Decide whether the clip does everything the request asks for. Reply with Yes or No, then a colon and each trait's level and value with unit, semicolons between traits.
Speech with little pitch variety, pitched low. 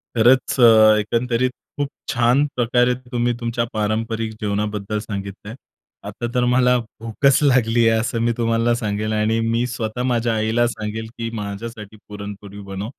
Yes: narrow, 2.1 semitones; low, 115 Hz